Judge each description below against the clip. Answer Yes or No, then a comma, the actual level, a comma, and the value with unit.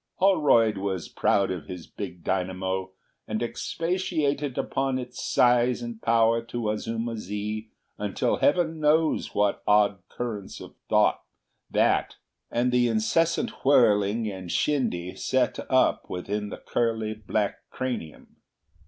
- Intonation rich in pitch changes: No, average, 3.8 semitones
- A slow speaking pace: Yes, slow, 125 wpm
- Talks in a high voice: No, low, 115 Hz